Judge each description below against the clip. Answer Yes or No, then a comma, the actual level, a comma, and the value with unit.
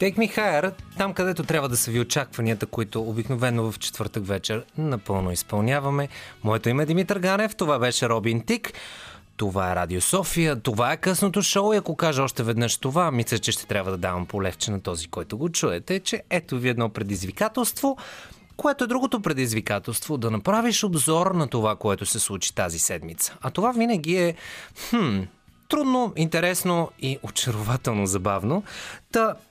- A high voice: No, low, 135 Hz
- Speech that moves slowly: No, fast, 165 wpm